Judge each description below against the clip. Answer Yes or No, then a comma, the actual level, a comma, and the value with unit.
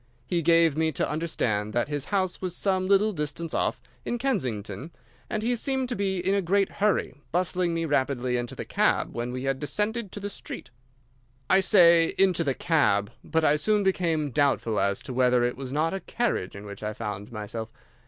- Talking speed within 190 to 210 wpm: Yes, average, 200 wpm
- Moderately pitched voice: Yes, medium, 160 Hz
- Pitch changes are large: Yes, wide, 7.4 semitones